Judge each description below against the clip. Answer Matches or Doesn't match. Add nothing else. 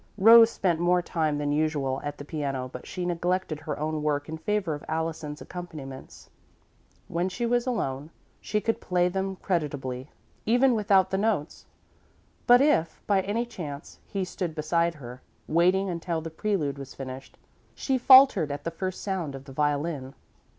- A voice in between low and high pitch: Matches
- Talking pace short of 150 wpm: Doesn't match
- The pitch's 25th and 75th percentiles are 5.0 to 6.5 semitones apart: Doesn't match